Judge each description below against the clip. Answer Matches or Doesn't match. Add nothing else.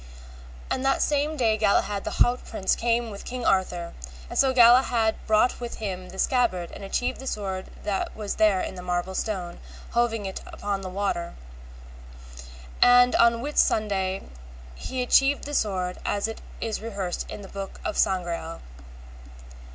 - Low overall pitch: Doesn't match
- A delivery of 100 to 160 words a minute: Matches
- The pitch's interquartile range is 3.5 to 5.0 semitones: Matches